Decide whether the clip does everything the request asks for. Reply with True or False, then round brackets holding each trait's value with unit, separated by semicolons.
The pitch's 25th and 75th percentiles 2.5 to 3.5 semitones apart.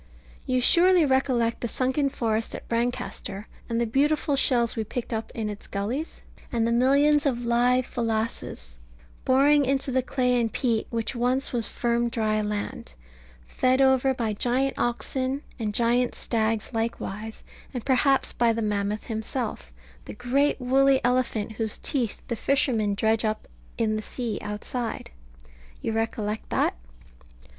True (2.9 semitones)